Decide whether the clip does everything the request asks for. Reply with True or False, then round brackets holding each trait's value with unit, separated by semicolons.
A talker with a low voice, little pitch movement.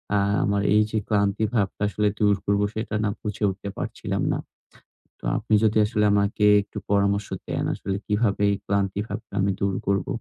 True (100 Hz; 1.0 semitones)